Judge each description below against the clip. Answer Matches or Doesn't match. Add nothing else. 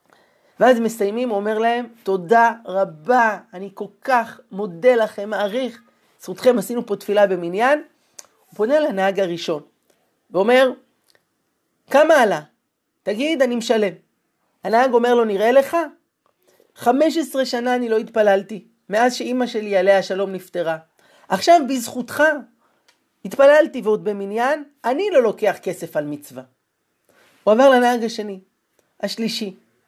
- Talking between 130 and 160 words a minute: Doesn't match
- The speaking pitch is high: Matches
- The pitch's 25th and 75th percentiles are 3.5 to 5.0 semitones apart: Matches